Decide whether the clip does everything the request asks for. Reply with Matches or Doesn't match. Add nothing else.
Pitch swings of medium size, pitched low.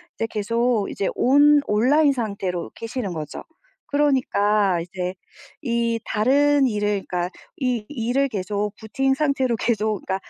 Doesn't match